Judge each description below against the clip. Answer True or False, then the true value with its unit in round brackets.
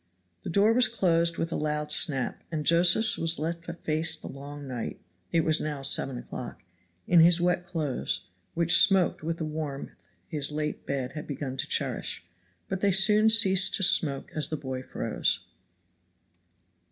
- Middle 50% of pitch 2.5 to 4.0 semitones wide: True (3.4 semitones)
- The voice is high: False (160 Hz)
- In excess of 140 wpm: True (170 wpm)